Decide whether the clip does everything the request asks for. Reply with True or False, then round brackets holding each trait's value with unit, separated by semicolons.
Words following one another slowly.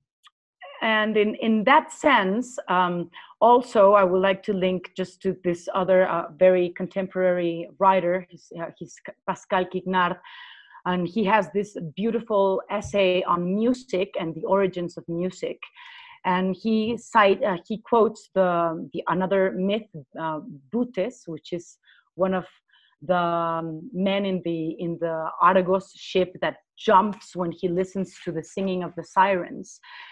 False (145 wpm)